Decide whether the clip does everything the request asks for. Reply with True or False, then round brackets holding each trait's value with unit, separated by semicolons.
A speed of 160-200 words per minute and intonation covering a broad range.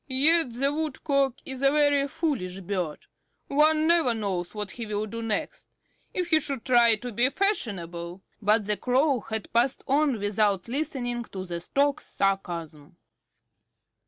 False (150 wpm; 5.8 semitones)